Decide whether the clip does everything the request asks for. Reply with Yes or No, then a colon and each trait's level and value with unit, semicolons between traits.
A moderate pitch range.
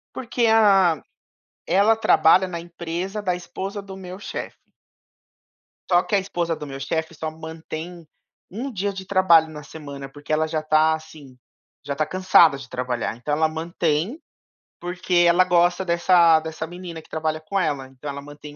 Yes: average, 3.1 semitones